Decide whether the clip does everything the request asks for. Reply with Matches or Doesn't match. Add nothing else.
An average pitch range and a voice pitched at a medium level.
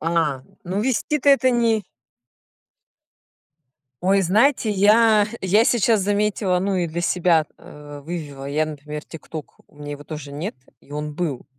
Doesn't match